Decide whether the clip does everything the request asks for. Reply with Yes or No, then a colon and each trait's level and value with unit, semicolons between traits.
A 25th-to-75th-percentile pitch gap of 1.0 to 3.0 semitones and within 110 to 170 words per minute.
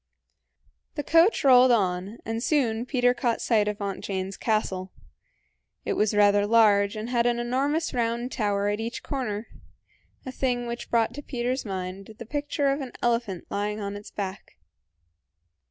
No: average, 3.4 semitones; average, 160 wpm